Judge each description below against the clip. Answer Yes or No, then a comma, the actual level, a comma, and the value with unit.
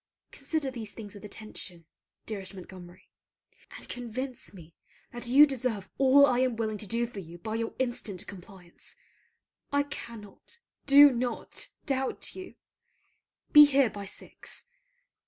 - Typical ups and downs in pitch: Yes, average, 4.7 semitones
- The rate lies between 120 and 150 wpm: Yes, average, 140 wpm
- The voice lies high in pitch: Yes, high, 230 Hz